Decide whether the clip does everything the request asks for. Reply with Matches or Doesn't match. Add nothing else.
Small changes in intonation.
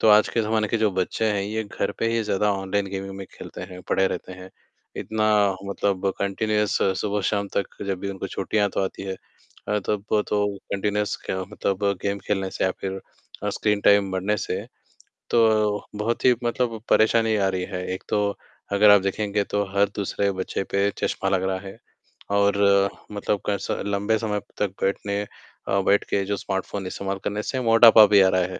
Matches